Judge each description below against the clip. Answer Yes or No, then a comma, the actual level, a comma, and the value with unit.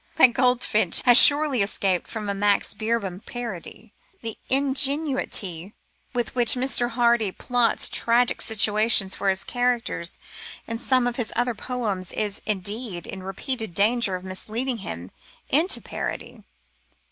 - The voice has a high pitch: Yes, high, 230 Hz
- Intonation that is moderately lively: Yes, average, 3.8 semitones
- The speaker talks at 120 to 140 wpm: Yes, slow, 135 wpm